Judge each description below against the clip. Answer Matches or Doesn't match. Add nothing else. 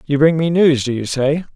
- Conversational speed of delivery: Doesn't match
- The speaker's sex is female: Doesn't match